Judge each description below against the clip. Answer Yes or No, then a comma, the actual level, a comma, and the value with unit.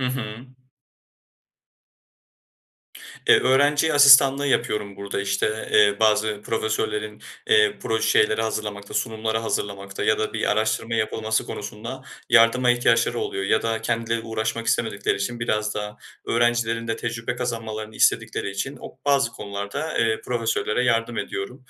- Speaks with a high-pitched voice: No, low, 115 Hz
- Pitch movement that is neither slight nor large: No, narrow, 2.2 semitones